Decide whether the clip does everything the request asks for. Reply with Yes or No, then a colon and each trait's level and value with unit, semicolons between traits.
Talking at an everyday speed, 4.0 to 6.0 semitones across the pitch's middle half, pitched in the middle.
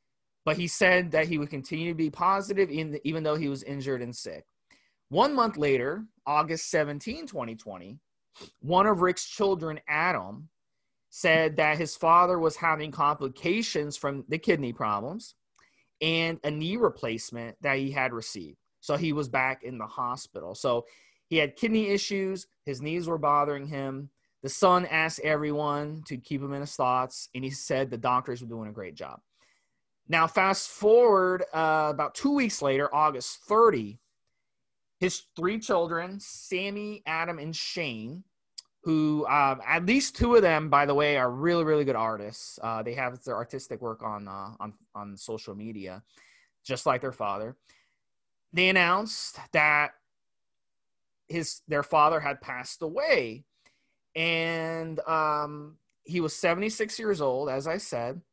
Yes: average, 155 wpm; average, 4.5 semitones; medium, 150 Hz